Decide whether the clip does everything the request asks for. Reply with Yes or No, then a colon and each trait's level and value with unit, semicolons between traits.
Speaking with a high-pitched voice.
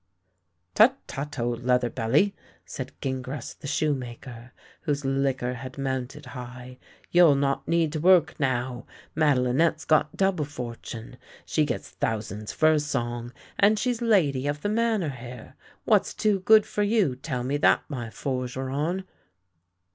No: low, 135 Hz